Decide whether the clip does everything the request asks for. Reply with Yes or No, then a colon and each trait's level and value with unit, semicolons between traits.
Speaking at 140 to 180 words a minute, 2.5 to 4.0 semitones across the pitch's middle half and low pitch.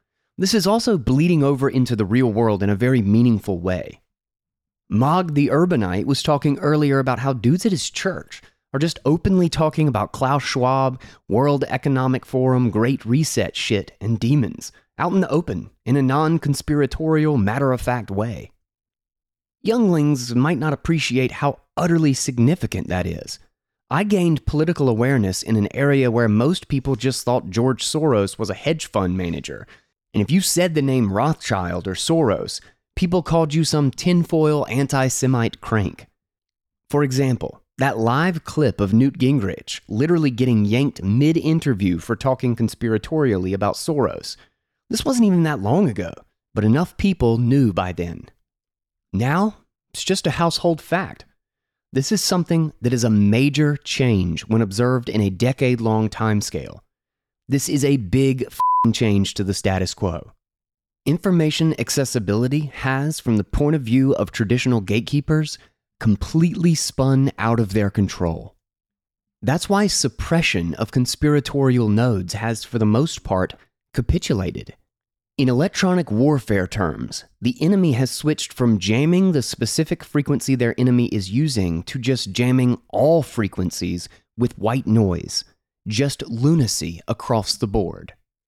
No: average, 145 wpm; wide, 5.6 semitones; low, 130 Hz